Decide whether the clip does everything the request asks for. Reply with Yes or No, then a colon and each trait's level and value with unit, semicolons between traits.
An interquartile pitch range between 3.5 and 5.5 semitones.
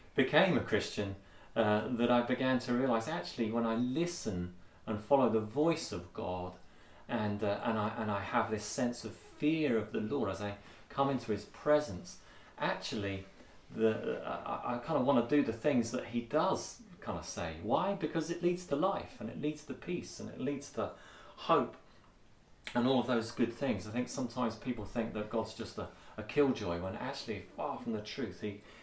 Yes: average, 4.0 semitones